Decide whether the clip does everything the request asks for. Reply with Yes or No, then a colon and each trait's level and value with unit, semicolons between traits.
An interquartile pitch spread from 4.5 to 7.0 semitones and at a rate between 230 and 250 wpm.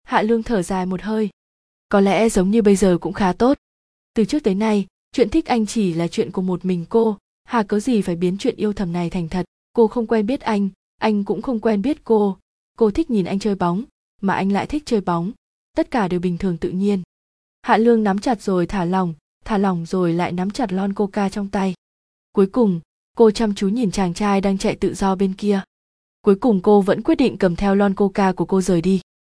No: average, 3.2 semitones; average, 235 wpm